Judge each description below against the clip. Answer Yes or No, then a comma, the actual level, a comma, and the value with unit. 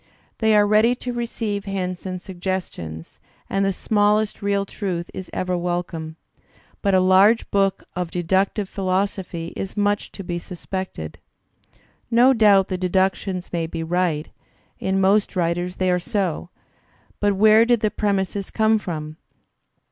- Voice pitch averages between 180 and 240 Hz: Yes, high, 190 Hz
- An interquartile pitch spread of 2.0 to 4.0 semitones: Yes, narrow, 2.5 semitones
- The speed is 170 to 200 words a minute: No, average, 150 wpm